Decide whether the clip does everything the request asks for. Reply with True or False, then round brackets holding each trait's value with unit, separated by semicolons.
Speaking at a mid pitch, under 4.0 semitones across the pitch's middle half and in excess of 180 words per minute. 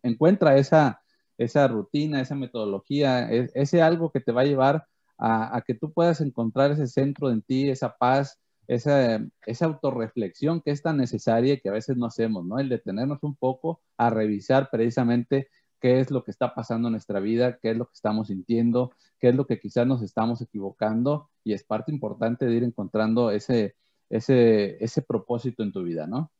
False (125 Hz; 3.5 semitones; 190 wpm)